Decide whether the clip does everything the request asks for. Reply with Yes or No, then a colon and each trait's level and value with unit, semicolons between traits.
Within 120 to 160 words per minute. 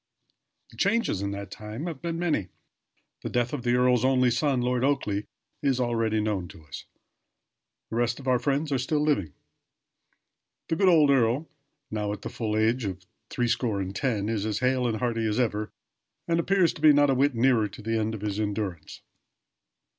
No: average, 195 wpm